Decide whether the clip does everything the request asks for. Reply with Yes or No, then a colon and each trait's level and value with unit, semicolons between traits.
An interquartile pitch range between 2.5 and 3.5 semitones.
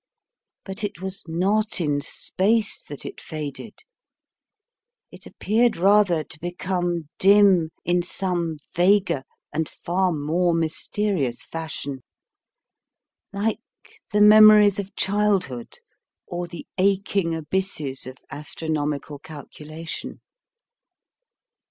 No: average, 4.3 semitones